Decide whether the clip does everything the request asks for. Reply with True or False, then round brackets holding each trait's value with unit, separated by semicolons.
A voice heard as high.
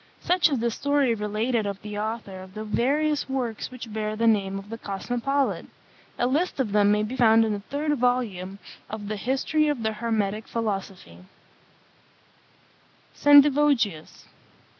True (225 Hz)